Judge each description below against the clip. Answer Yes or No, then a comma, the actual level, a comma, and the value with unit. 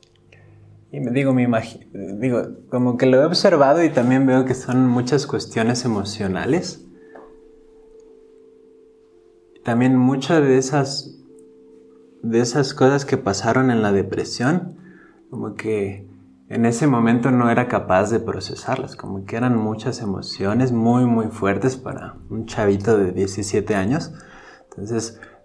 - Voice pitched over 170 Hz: No, low, 120 Hz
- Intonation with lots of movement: No, average, 4.3 semitones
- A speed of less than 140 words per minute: Yes, average, 130 wpm